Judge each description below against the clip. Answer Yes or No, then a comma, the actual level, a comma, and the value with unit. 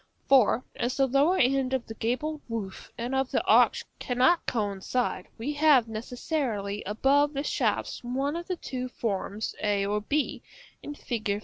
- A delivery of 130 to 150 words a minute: No, average, 165 wpm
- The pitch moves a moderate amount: Yes, average, 4.4 semitones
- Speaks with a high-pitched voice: Yes, very high, 250 Hz